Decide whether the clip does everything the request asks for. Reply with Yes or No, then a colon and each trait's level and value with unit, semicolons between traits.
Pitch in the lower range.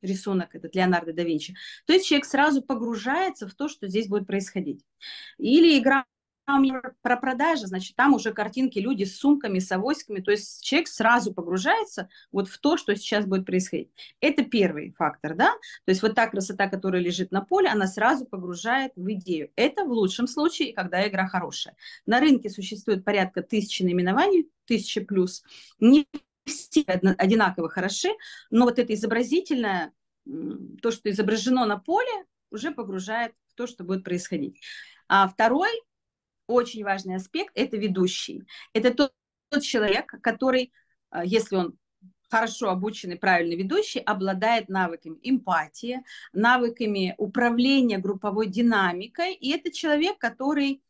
No: high, 225 Hz